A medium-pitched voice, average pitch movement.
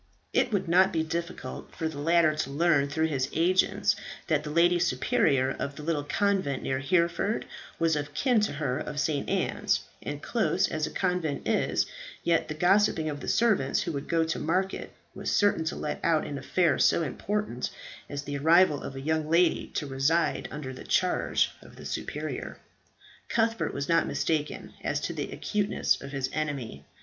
Yes: medium, 160 Hz; average, 3.7 semitones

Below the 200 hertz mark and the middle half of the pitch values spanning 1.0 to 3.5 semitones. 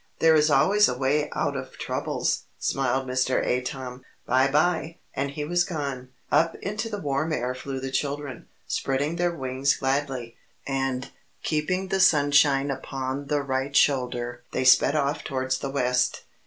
Yes: medium, 140 Hz; narrow, 2.5 semitones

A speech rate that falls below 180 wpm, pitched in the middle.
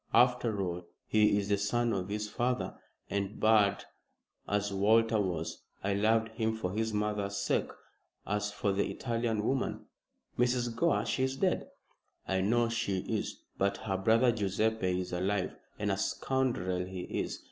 No: average, 160 wpm; low, 105 Hz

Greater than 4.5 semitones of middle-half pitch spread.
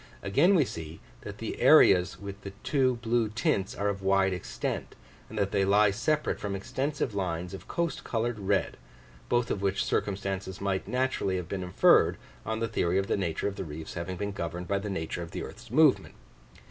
No: average, 3.3 semitones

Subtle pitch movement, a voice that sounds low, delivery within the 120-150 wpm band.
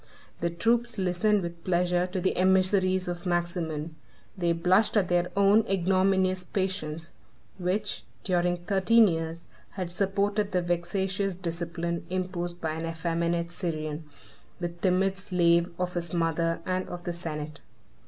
No: narrow, 1.9 semitones; medium, 180 Hz; slow, 135 wpm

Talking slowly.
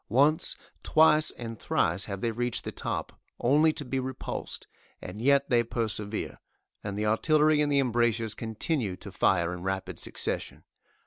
No: average, 155 wpm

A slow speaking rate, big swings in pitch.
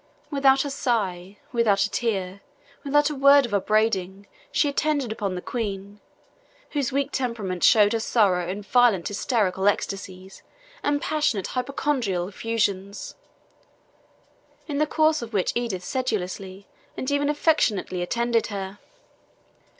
Yes: slow, 125 wpm; wide, 5.7 semitones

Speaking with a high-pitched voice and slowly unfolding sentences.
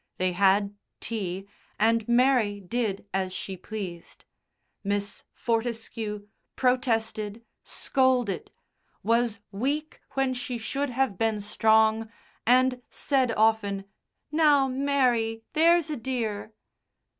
Yes: high, 225 Hz; slow, 100 wpm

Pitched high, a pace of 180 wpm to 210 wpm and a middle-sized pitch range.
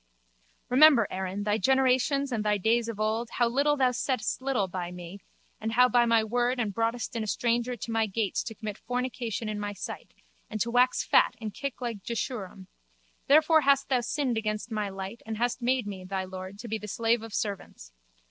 Yes: high, 225 Hz; average, 195 wpm; average, 3.2 semitones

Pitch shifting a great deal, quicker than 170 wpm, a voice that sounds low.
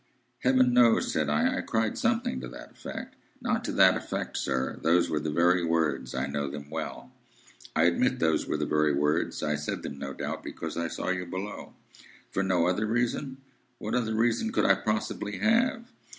Yes: wide, 7.2 semitones; average, 190 wpm; very low, 85 Hz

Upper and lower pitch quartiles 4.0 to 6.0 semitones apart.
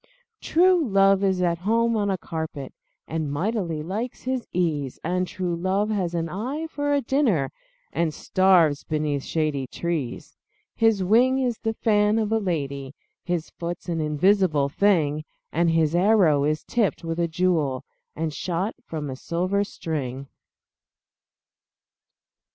Yes: average, 5.1 semitones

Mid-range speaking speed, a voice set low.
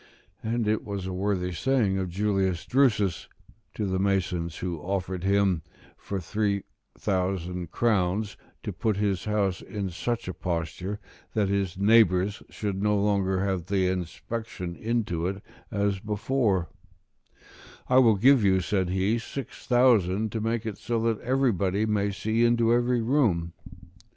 Yes: average, 150 wpm; low, 100 Hz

